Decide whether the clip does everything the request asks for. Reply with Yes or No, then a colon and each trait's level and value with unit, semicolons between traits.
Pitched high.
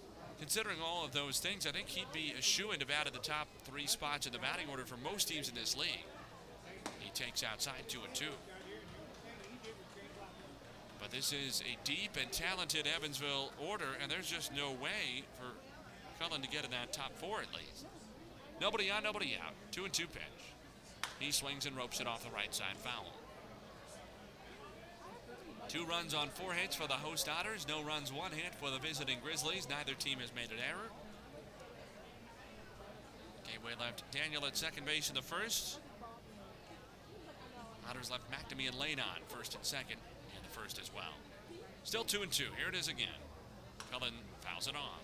No: medium, 145 Hz